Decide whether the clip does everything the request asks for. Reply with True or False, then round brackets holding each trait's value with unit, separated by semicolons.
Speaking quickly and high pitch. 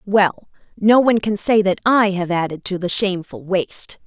False (190 wpm; 195 Hz)